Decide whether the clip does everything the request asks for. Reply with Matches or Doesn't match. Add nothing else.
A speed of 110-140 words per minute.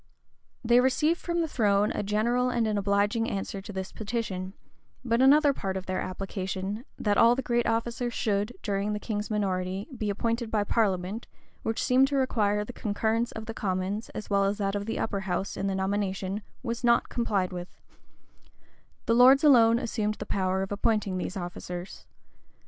Doesn't match